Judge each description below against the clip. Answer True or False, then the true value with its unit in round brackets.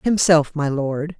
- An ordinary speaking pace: True (150 wpm)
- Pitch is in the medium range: True (155 Hz)